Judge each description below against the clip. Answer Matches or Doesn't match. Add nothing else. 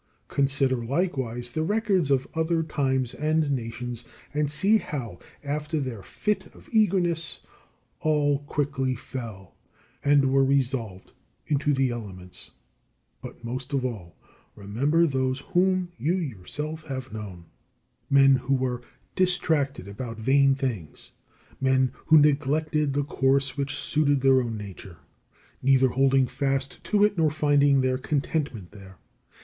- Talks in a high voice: Doesn't match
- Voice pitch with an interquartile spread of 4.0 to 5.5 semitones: Doesn't match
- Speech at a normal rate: Doesn't match